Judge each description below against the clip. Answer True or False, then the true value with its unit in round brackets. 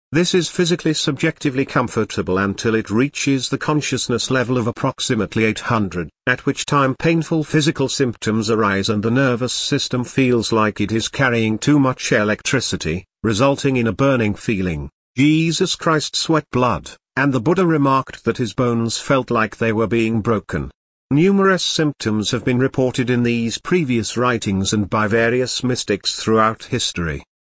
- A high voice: False (125 Hz)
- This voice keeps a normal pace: True (150 wpm)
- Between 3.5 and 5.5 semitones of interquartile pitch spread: True (4.0 semitones)